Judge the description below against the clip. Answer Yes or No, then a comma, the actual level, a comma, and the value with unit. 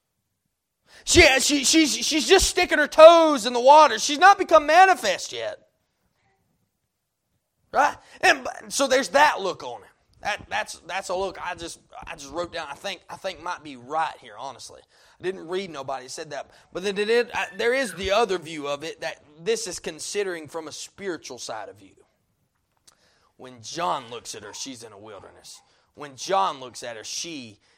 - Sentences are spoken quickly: No, average, 190 wpm